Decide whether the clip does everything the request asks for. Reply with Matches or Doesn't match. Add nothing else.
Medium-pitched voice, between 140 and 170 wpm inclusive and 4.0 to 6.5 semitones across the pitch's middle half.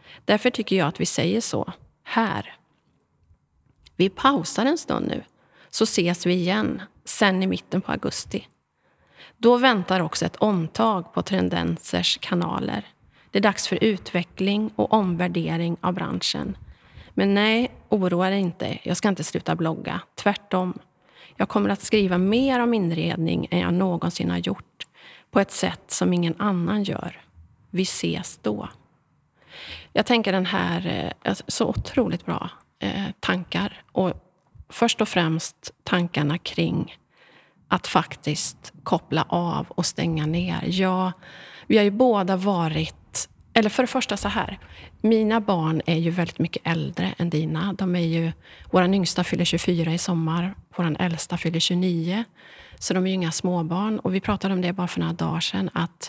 Doesn't match